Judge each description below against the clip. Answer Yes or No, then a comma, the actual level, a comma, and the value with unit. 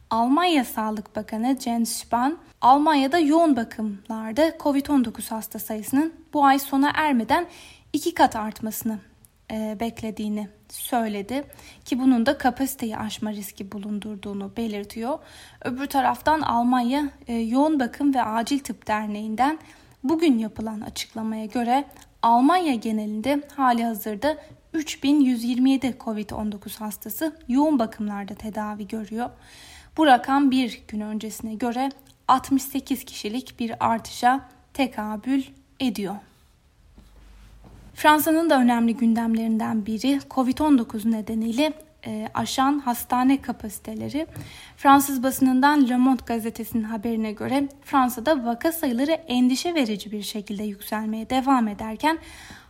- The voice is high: Yes, high, 245 Hz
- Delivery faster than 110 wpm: No, average, 105 wpm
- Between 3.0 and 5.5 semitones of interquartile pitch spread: Yes, average, 4.0 semitones